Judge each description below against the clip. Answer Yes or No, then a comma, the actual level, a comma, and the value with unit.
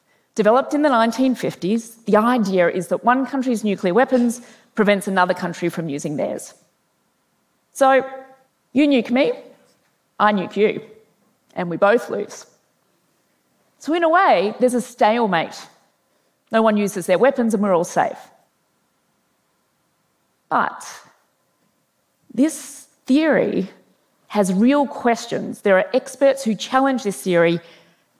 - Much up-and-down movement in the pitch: No, average, 4.9 semitones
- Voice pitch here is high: Yes, high, 230 Hz